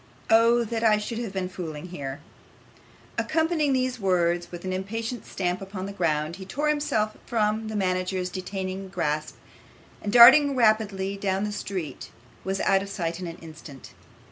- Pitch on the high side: Yes, high, 195 Hz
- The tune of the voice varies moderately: Yes, average, 3.7 semitones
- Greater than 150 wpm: Yes, average, 165 wpm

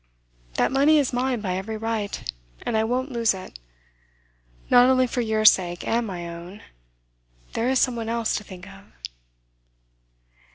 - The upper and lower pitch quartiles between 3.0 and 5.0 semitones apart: Yes, average, 4.2 semitones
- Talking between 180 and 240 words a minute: No, average, 160 wpm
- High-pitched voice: Yes, high, 225 Hz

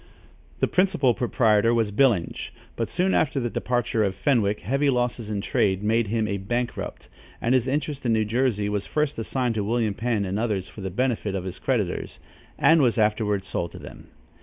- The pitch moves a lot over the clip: No, average, 3.5 semitones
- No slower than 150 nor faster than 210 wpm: Yes, average, 190 wpm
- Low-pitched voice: Yes, low, 115 Hz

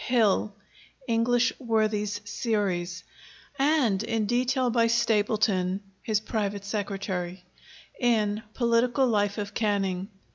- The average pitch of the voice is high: Yes, high, 215 Hz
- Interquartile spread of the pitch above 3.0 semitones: No, average, 2.7 semitones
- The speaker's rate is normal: No, slow, 100 wpm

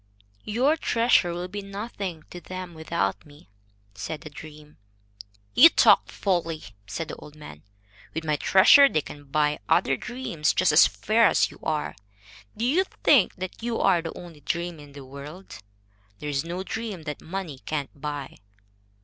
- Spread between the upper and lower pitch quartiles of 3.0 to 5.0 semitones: Yes, average, 4.7 semitones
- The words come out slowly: No, average, 165 wpm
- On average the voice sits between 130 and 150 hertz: No, medium, 165 Hz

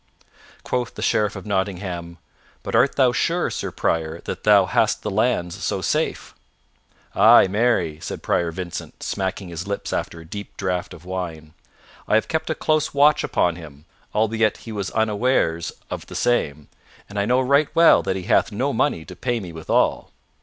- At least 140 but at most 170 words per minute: No, average, 180 wpm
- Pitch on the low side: Yes, low, 100 Hz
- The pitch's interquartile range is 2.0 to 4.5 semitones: No, wide, 5.6 semitones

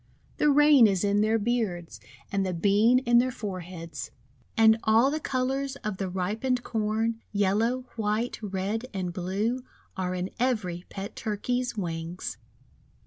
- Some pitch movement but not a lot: Yes, average, 4.4 semitones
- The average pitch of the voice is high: Yes, high, 215 Hz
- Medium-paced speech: Yes, average, 150 wpm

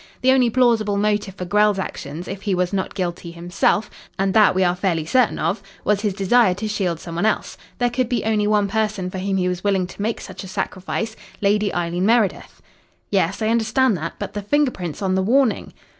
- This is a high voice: Yes, high, 200 Hz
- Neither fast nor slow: No, fast, 220 wpm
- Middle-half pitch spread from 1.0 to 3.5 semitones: Yes, average, 3.1 semitones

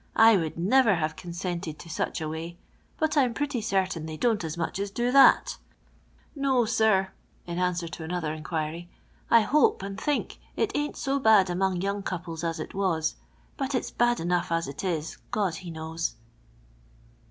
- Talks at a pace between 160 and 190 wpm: Yes, average, 180 wpm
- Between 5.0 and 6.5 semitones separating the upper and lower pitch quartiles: Yes, wide, 5.5 semitones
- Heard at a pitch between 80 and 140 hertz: No, medium, 185 Hz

